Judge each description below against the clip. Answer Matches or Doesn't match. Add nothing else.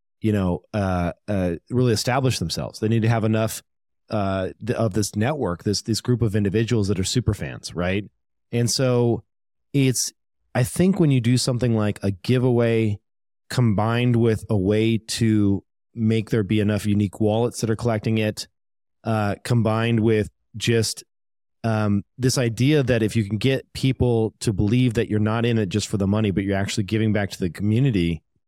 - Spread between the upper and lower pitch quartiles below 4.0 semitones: Matches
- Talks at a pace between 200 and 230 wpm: Doesn't match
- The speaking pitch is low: Matches